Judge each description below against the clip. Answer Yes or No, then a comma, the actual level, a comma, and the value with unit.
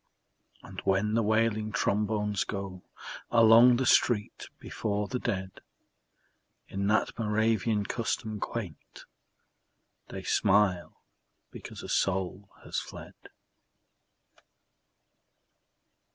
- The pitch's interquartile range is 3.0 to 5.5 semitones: No, narrow, 2.4 semitones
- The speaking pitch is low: Yes, low, 105 Hz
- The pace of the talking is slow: Yes, slow, 90 wpm